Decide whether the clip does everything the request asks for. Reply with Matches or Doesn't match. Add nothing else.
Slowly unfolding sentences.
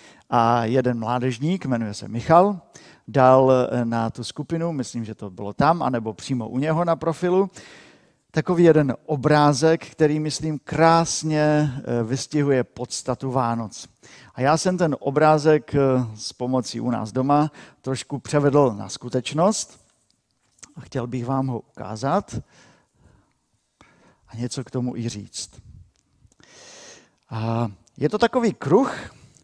Doesn't match